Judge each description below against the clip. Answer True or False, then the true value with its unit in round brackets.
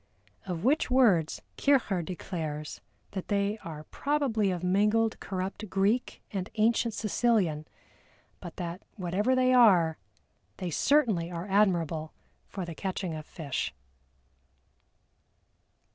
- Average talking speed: False (115 wpm)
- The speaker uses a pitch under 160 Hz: False (190 Hz)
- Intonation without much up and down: False (4.8 semitones)